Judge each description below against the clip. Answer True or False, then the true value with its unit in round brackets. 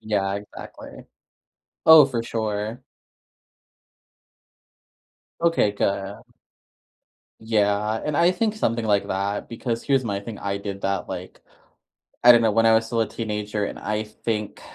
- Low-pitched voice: True (110 Hz)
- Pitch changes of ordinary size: False (2.3 semitones)